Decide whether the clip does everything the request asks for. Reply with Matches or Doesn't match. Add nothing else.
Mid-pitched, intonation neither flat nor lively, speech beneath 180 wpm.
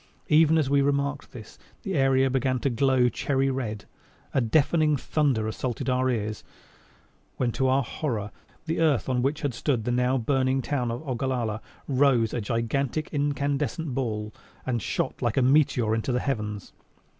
Doesn't match